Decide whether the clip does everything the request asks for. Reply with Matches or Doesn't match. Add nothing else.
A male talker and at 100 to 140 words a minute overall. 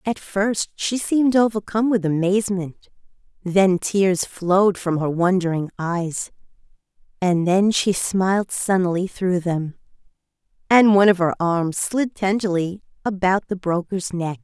Doesn't match